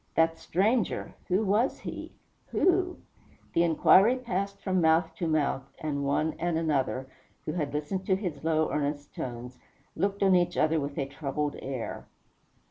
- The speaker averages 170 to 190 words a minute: No, average, 155 wpm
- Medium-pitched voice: Yes, medium, 165 Hz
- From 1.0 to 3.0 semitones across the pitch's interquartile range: No, average, 4.7 semitones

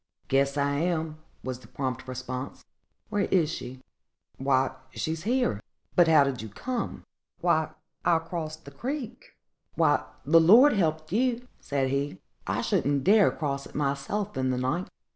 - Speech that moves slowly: No, average, 150 wpm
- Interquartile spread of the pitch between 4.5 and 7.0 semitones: Yes, average, 5.3 semitones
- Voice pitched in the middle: Yes, medium, 155 Hz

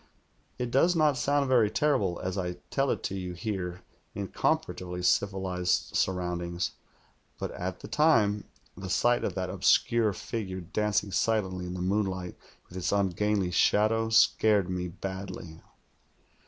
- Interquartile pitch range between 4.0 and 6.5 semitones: No, average, 3.4 semitones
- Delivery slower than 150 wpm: Yes, average, 140 wpm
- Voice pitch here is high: No, very low, 95 Hz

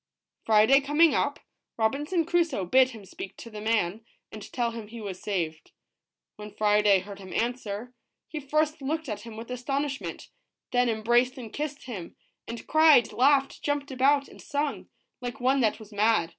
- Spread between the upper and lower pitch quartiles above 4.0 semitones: Yes, average, 4.9 semitones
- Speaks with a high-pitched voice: Yes, high, 240 Hz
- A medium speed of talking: Yes, average, 170 wpm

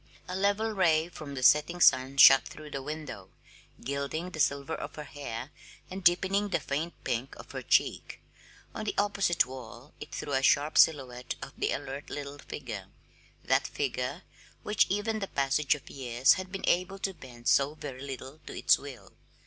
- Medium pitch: Yes, medium, 145 Hz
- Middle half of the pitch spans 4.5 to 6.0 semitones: Yes, average, 5.0 semitones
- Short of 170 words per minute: No, average, 180 wpm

